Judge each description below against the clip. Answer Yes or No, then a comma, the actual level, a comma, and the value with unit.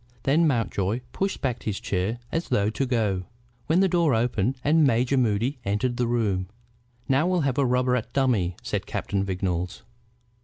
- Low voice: Yes, low, 120 Hz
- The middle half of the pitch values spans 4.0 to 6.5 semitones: Yes, average, 5.2 semitones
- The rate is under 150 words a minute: No, average, 170 wpm